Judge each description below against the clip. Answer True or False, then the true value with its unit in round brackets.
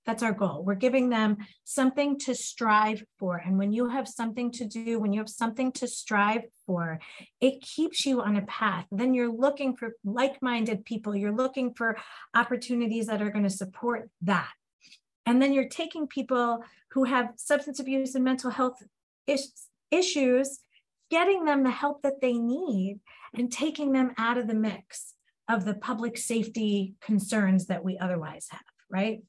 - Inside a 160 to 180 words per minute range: True (175 wpm)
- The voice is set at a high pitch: True (235 Hz)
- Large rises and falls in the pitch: False (3.8 semitones)